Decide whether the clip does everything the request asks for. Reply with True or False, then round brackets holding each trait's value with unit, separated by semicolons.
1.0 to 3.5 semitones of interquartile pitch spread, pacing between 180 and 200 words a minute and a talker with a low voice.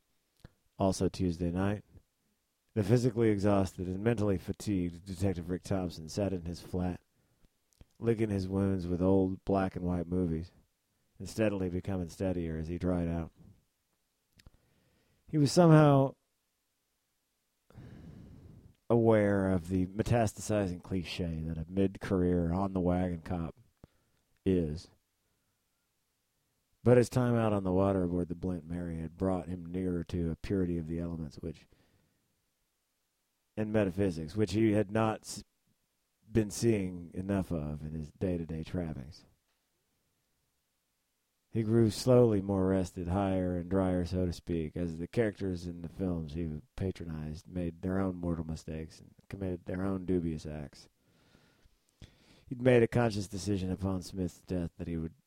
False (2.8 semitones; 140 wpm; 95 Hz)